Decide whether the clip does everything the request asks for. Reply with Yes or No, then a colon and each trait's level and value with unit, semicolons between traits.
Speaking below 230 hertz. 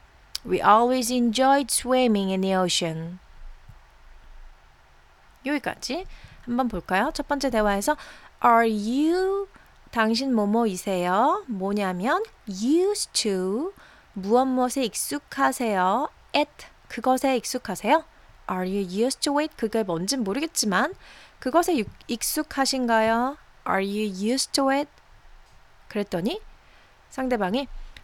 No: high, 235 Hz